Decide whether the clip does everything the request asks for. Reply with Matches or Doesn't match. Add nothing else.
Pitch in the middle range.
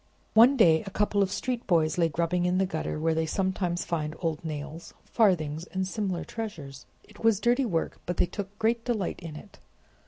Matches